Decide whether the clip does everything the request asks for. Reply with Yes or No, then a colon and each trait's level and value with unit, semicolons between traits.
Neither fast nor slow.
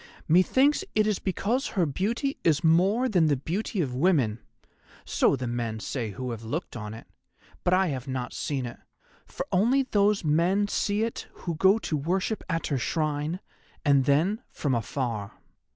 Yes: average, 170 wpm